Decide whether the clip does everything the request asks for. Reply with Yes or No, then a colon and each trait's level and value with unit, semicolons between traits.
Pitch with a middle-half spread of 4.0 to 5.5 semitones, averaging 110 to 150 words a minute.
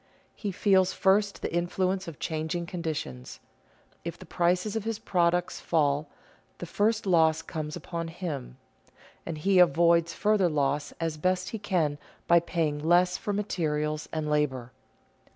No: average, 3.4 semitones; average, 145 wpm